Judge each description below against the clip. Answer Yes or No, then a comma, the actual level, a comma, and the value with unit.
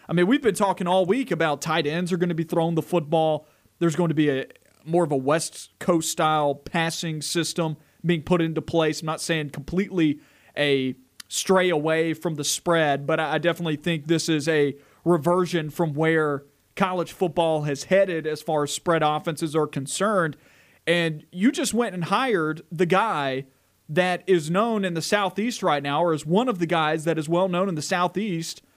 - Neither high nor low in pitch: Yes, medium, 165 Hz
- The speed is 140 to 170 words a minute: No, average, 195 wpm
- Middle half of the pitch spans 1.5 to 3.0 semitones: Yes, average, 2.7 semitones